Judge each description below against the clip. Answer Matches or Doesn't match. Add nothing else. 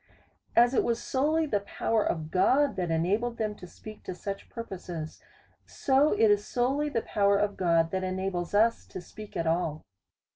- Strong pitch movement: Doesn't match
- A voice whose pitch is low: Doesn't match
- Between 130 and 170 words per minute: Doesn't match